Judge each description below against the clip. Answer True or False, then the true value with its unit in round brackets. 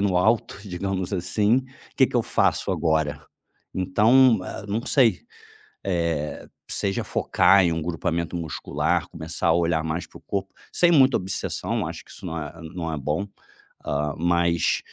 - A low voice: True (90 Hz)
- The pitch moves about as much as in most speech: True (3.6 semitones)